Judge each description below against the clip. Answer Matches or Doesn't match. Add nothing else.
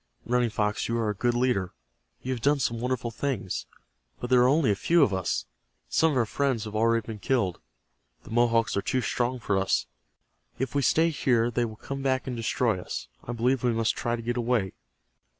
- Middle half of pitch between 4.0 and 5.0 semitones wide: Doesn't match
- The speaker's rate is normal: Doesn't match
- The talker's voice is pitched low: Matches